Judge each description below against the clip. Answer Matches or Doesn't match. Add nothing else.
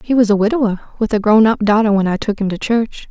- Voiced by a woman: Matches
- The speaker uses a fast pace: Matches